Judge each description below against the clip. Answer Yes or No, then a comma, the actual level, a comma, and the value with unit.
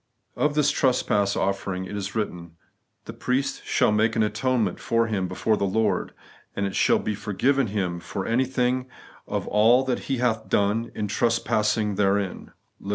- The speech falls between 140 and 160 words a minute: No, average, 175 wpm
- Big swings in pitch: No, average, 3.7 semitones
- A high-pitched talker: No, low, 110 Hz